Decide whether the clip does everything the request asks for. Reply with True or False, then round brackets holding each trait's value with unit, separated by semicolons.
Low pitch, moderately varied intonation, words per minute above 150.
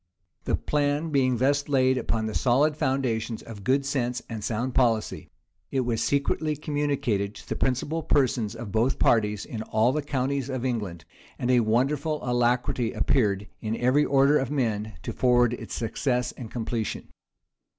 True (125 Hz; 3.7 semitones; 160 wpm)